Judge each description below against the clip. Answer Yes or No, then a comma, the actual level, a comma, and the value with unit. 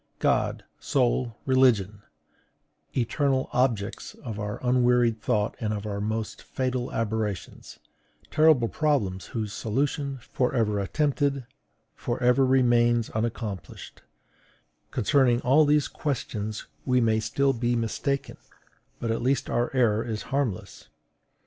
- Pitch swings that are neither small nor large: Yes, average, 3.3 semitones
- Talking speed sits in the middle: No, slow, 115 wpm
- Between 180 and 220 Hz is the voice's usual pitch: No, low, 120 Hz